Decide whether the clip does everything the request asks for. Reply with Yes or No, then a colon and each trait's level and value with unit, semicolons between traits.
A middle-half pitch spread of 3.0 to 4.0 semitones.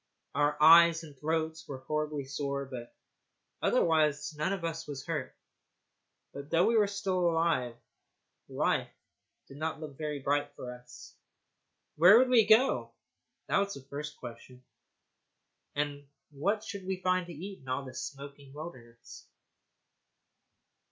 Yes: average, 3.5 semitones